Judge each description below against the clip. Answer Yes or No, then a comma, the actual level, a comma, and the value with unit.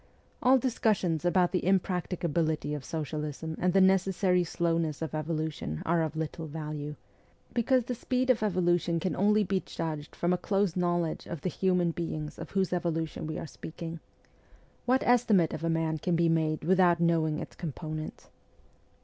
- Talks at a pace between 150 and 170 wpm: Yes, average, 165 wpm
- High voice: No, medium, 170 Hz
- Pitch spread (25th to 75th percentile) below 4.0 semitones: Yes, average, 2.9 semitones